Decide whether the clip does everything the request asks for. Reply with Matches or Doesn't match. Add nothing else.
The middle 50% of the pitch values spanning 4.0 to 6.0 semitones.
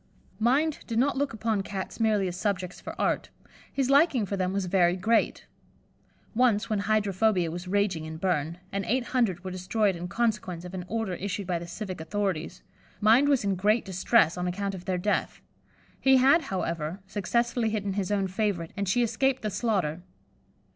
Doesn't match